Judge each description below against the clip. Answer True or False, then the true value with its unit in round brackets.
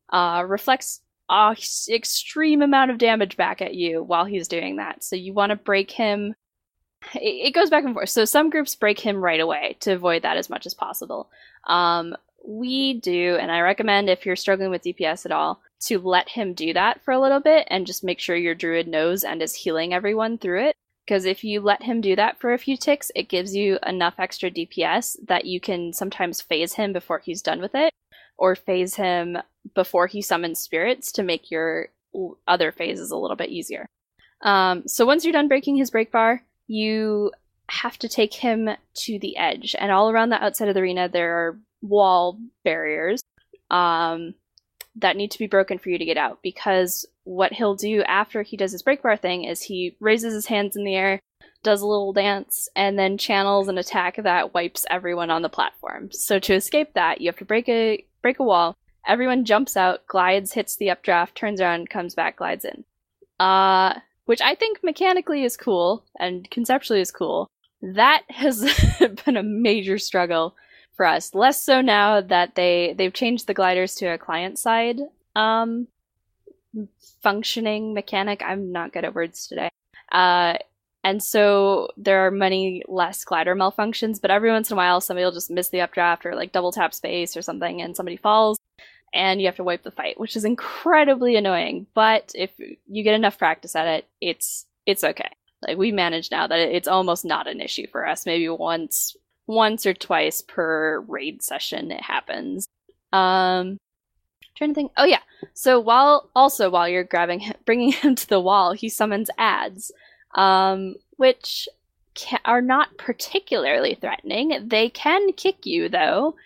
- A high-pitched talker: True (200 Hz)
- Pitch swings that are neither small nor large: True (4.3 semitones)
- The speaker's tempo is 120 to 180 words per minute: False (190 wpm)